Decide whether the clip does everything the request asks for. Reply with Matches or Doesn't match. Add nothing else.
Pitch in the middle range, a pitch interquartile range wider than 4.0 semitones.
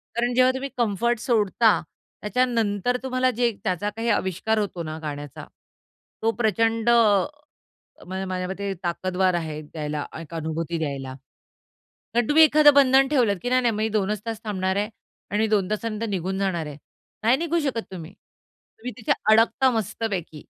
Doesn't match